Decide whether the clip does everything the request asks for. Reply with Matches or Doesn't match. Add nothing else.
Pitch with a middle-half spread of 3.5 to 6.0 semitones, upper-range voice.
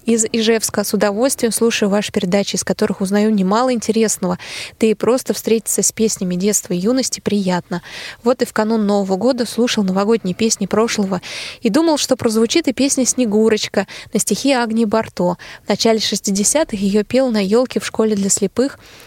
Doesn't match